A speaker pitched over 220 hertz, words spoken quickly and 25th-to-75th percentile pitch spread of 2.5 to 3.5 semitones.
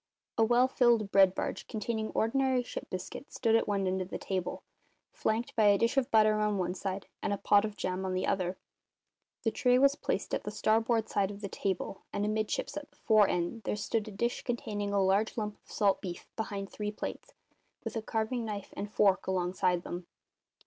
No: high, 210 Hz; fast, 210 wpm; average, 2.8 semitones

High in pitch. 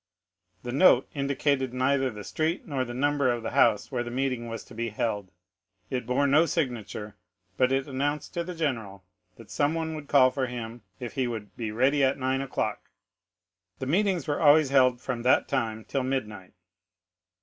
No: low, 130 Hz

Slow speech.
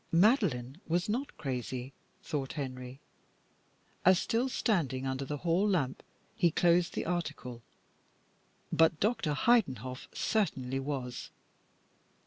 Yes: slow, 110 wpm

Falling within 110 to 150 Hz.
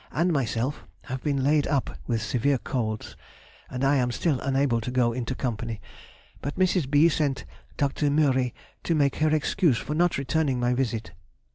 Yes: low, 135 Hz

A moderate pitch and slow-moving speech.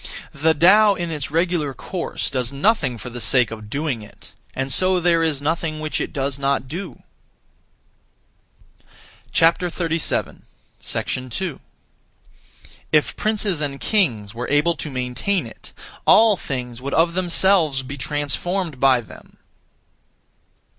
Yes: medium, 150 Hz; slow, 125 wpm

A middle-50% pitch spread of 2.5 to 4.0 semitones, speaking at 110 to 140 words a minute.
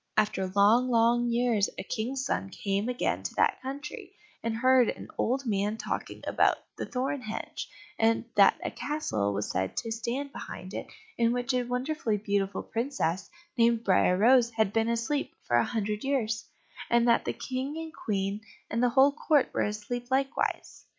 No: average, 3.6 semitones; average, 175 wpm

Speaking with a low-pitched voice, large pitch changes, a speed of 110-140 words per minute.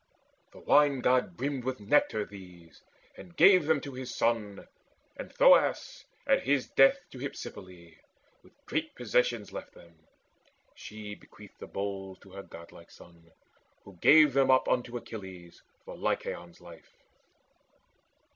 Yes: low, 115 Hz; wide, 7.0 semitones; slow, 135 wpm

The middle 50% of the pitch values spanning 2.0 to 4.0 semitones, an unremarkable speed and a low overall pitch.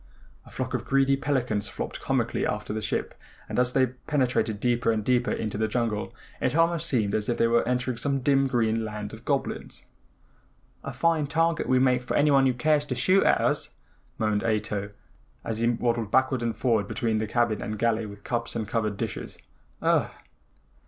Yes: average, 3.4 semitones; average, 190 wpm; low, 120 Hz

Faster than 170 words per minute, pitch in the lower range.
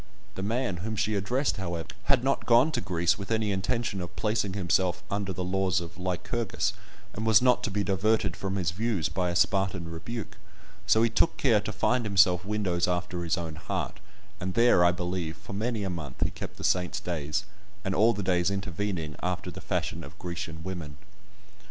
Yes: average, 195 wpm; very low, 95 Hz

